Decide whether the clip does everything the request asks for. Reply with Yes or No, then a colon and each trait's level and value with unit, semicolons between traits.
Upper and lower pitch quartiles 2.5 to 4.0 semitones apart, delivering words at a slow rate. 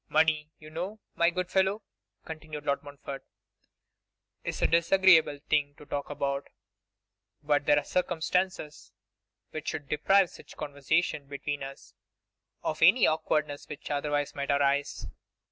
Yes: average, 2.9 semitones; slow, 130 wpm